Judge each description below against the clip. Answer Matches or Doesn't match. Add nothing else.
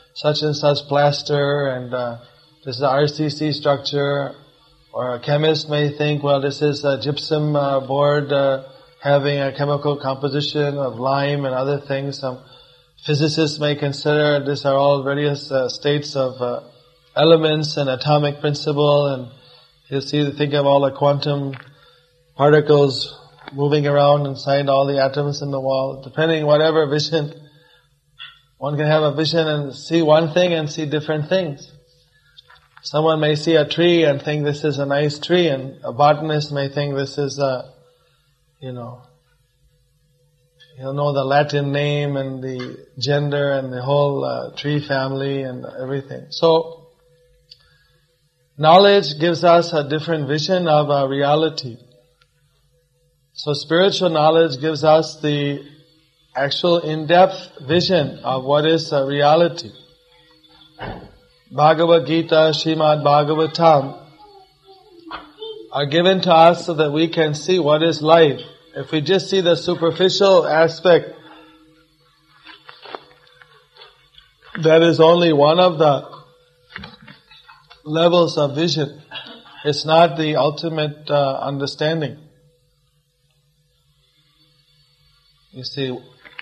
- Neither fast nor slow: Doesn't match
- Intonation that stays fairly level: Matches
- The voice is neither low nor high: Matches